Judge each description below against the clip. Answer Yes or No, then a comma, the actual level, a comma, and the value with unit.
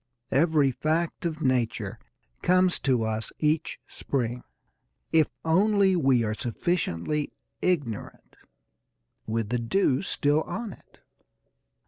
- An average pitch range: No, wide, 6.1 semitones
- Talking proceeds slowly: Yes, slow, 105 wpm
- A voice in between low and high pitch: Yes, medium, 150 Hz